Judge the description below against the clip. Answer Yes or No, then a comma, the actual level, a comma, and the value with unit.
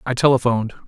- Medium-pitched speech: No, low, 125 Hz